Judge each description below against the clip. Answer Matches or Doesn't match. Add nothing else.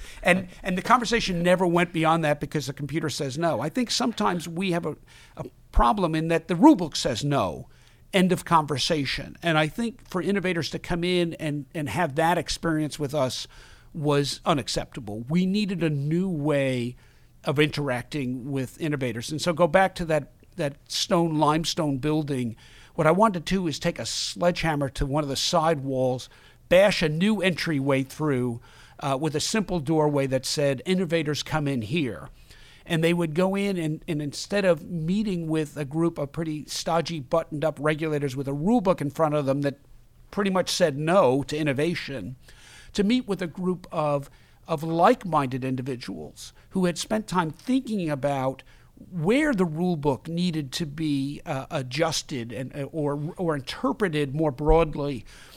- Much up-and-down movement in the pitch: Doesn't match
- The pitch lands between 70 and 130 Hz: Doesn't match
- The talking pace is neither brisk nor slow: Matches